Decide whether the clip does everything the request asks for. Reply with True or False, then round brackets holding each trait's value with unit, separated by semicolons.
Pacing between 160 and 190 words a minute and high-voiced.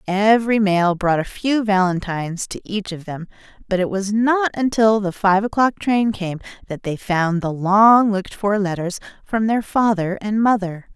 True (180 wpm; 200 Hz)